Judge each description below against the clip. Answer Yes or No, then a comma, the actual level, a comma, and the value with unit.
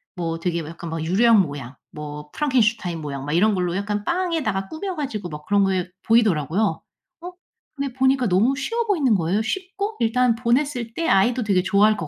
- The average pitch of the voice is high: Yes, high, 210 Hz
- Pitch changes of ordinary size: No, wide, 7.0 semitones